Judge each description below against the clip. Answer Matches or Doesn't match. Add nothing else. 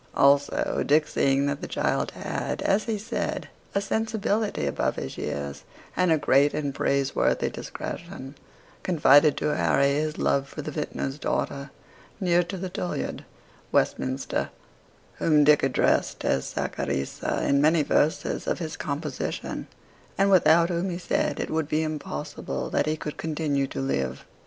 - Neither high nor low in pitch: Matches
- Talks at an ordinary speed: Matches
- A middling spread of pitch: Matches